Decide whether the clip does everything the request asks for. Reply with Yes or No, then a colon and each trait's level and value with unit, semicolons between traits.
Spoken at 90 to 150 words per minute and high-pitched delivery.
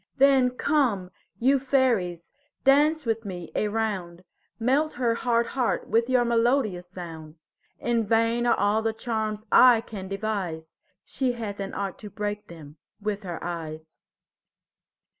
Yes: average, 140 wpm; high, 220 Hz